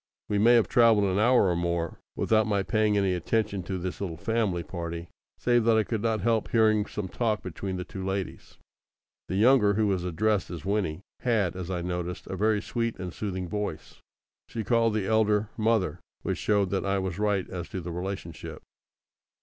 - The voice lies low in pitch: Yes, low, 100 Hz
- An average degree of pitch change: Yes, average, 3.1 semitones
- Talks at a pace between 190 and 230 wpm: Yes, average, 195 wpm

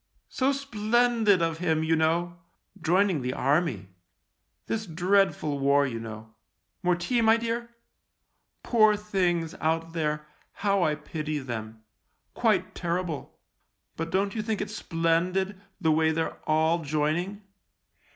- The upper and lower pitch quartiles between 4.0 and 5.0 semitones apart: Yes, average, 4.7 semitones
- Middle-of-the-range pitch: Yes, medium, 170 Hz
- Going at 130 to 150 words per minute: Yes, average, 140 wpm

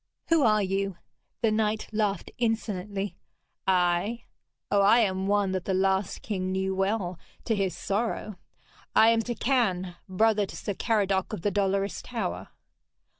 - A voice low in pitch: No, high, 200 Hz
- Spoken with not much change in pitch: Yes, narrow, 2.3 semitones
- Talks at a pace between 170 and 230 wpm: No, average, 145 wpm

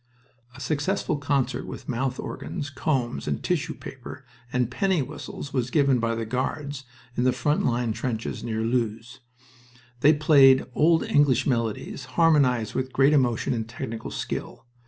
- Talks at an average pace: Yes, average, 150 wpm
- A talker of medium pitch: No, low, 130 Hz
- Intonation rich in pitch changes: No, average, 3.3 semitones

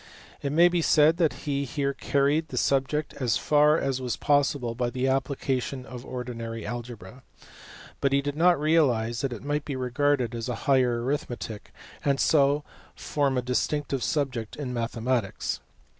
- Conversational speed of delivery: Yes, average, 160 wpm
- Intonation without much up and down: No, average, 3.0 semitones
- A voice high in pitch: No, low, 135 Hz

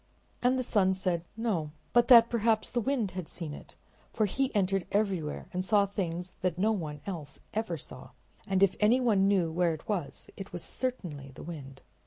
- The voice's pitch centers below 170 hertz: No, high, 190 Hz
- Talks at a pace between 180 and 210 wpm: Yes, average, 190 wpm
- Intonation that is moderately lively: Yes, average, 4.4 semitones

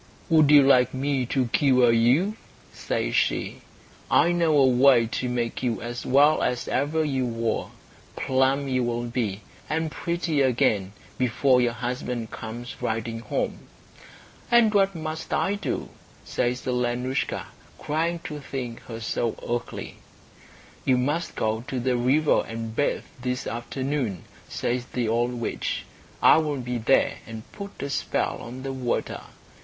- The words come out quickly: No, average, 150 wpm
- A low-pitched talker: Yes, low, 125 Hz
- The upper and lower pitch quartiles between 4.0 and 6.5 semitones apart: No, average, 3.4 semitones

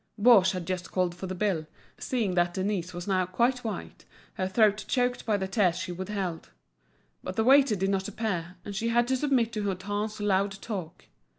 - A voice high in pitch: Yes, high, 200 Hz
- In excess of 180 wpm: Yes, average, 195 wpm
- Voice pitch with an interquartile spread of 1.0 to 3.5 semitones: Yes, average, 3.2 semitones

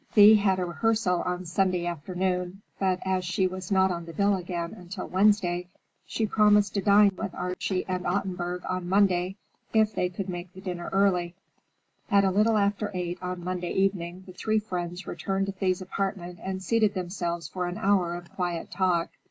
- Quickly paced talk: No, average, 185 wpm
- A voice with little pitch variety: Yes, narrow, 2.0 semitones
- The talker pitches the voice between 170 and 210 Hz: Yes, medium, 185 Hz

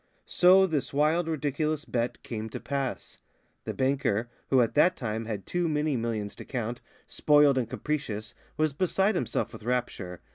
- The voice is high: No, low, 135 Hz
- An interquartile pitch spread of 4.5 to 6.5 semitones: Yes, average, 5.2 semitones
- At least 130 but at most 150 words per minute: No, average, 160 wpm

